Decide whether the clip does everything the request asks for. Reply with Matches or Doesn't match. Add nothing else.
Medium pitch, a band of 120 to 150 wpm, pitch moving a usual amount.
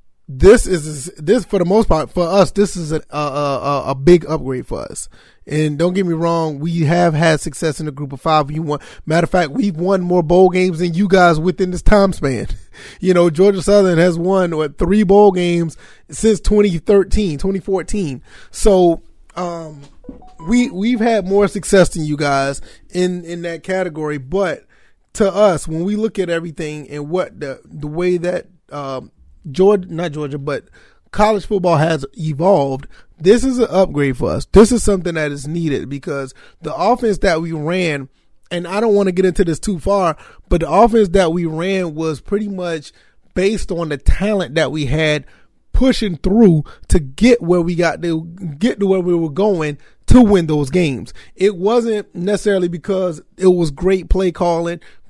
Doesn't match